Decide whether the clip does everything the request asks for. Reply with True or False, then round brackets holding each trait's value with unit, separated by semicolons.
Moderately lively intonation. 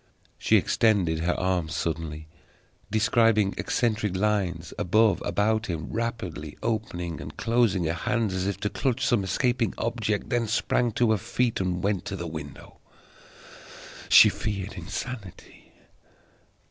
True (4.4 semitones)